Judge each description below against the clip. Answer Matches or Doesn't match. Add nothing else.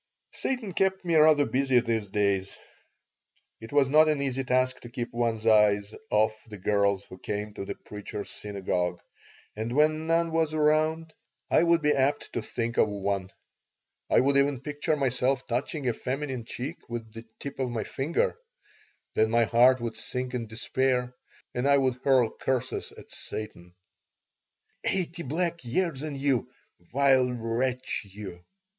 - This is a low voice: Matches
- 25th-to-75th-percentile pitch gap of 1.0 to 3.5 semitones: Doesn't match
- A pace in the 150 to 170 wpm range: Matches